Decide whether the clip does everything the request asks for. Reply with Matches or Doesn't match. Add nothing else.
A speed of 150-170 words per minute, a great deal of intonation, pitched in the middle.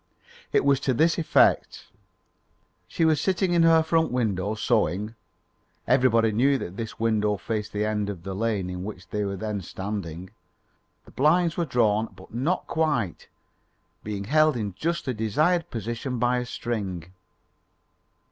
Doesn't match